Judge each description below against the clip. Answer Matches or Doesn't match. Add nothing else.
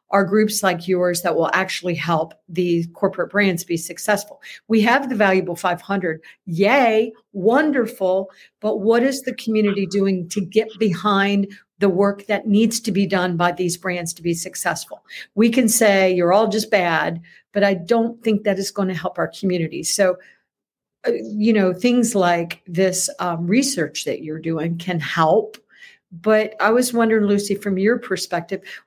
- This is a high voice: Matches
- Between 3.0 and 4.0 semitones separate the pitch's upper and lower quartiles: Matches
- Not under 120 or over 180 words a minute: Matches